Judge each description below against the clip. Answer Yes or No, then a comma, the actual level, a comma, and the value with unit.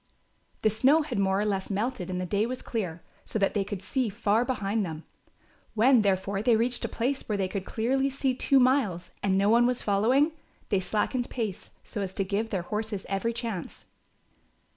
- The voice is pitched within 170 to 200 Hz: No, high, 215 Hz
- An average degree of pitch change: Yes, average, 3.8 semitones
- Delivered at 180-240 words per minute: Yes, average, 195 wpm